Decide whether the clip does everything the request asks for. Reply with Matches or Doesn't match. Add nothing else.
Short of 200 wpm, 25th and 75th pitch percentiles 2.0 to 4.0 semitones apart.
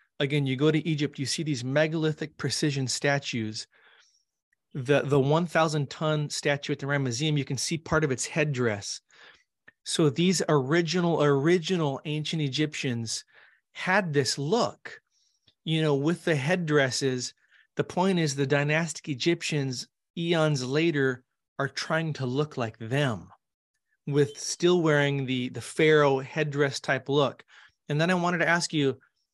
Matches